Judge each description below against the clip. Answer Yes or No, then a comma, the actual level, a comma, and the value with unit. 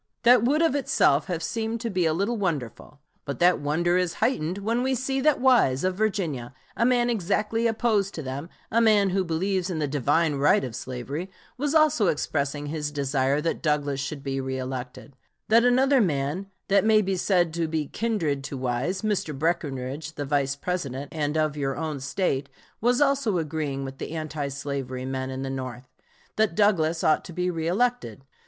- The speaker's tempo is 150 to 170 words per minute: No, average, 185 wpm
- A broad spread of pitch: Yes, wide, 7.0 semitones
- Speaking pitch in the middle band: Yes, medium, 160 Hz